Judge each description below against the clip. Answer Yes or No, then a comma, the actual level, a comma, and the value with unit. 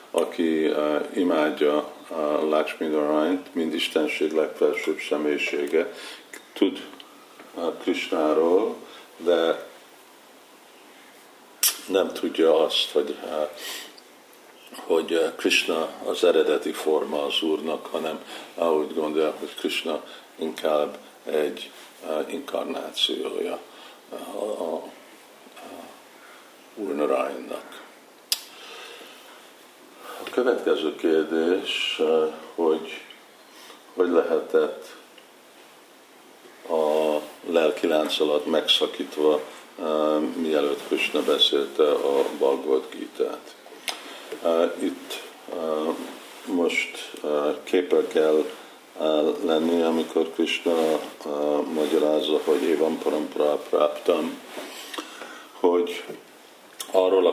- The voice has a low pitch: No, very high, 390 Hz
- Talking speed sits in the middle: No, slow, 75 wpm